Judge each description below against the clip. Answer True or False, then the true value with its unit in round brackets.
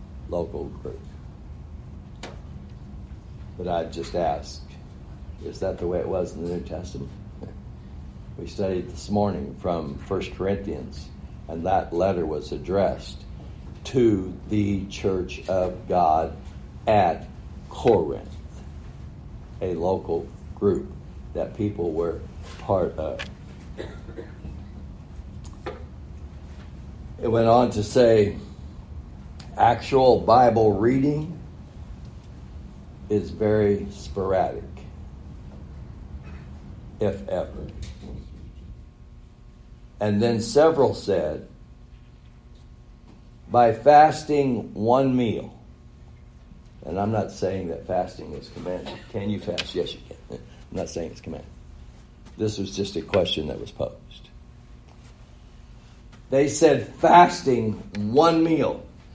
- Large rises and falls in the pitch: True (7.1 semitones)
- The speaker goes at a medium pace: False (95 wpm)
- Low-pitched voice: True (85 Hz)